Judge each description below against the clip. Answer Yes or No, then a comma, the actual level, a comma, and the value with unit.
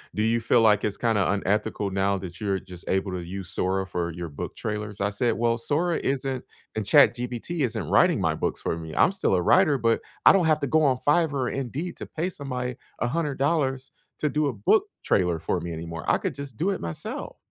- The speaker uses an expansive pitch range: Yes, wide, 6.6 semitones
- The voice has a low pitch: Yes, low, 115 Hz